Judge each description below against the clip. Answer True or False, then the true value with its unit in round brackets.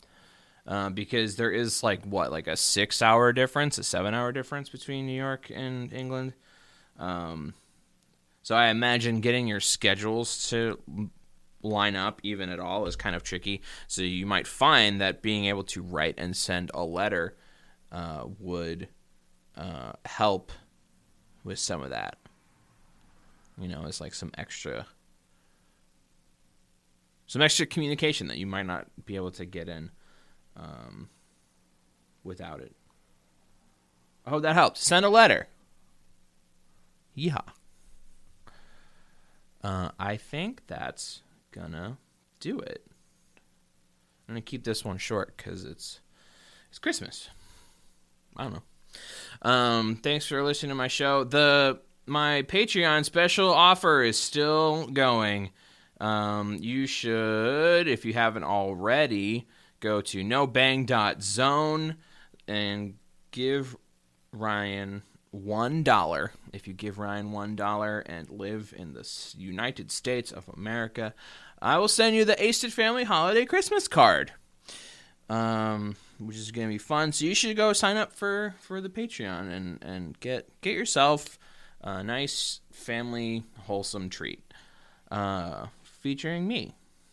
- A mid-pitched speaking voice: False (110 Hz)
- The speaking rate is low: True (130 wpm)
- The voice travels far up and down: True (6.7 semitones)